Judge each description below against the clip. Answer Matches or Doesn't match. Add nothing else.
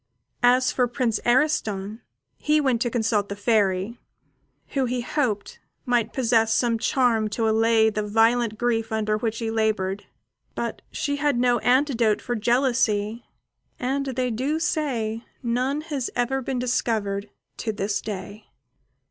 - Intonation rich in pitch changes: Doesn't match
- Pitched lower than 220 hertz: Doesn't match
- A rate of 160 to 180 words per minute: Doesn't match